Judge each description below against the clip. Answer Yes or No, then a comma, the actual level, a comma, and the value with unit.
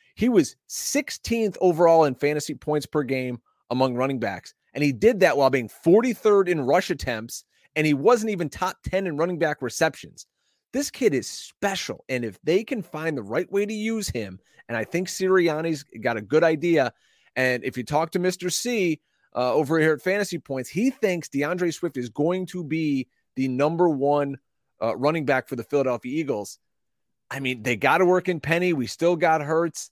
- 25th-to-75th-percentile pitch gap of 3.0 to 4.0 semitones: No, average, 5.3 semitones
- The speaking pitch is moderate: Yes, medium, 160 Hz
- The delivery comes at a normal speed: Yes, average, 195 wpm